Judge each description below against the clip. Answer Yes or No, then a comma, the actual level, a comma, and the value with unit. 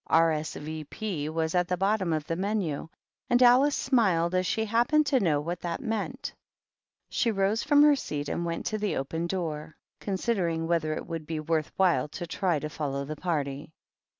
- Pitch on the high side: No, medium, 170 Hz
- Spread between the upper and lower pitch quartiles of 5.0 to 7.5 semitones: Yes, wide, 5.5 semitones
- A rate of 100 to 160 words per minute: No, average, 195 wpm